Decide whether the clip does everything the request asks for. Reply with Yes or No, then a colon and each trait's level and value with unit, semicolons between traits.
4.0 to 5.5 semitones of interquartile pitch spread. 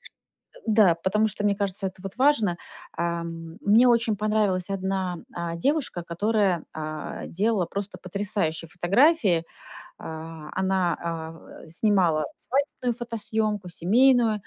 Yes: average, 4.3 semitones